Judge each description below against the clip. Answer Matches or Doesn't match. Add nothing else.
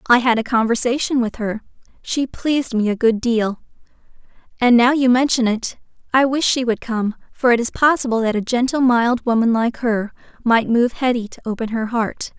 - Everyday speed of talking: Matches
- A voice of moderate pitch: Doesn't match